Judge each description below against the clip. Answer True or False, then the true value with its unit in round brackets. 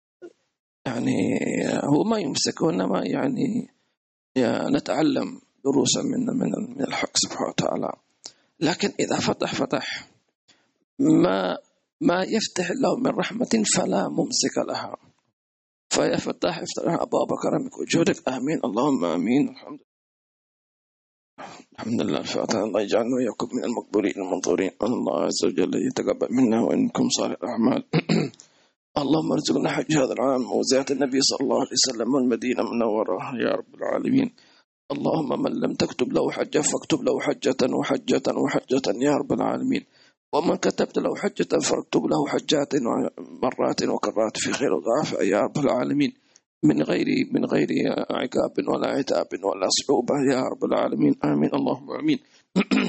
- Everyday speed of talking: False (130 wpm)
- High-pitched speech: True (250 Hz)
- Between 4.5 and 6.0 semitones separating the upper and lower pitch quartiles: False (3.5 semitones)